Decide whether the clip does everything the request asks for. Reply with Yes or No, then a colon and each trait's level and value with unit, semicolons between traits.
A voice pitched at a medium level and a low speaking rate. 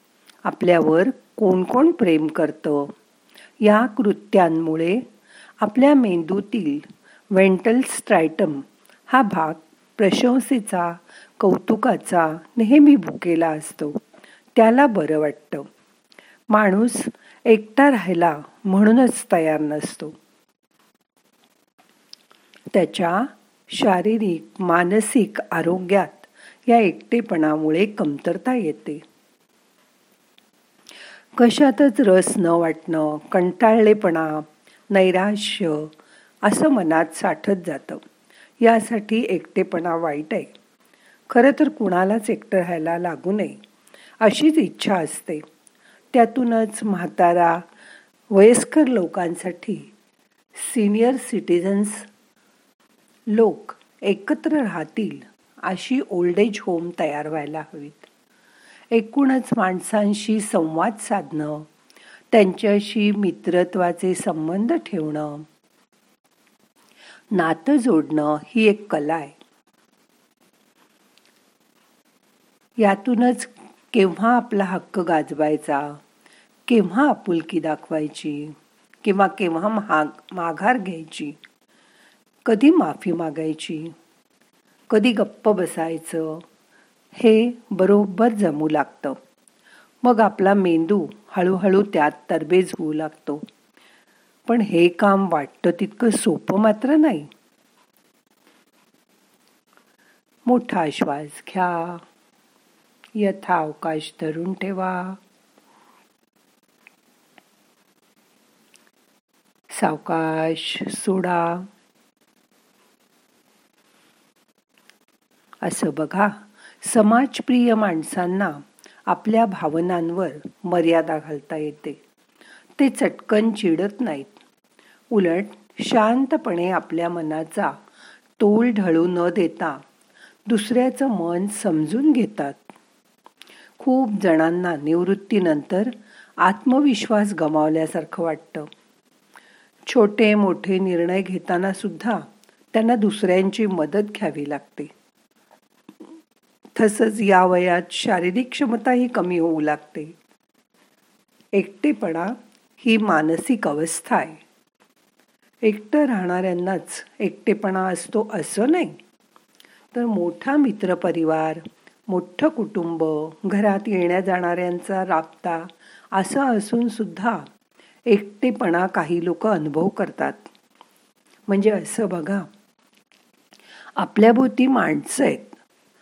No: high, 195 Hz; slow, 75 wpm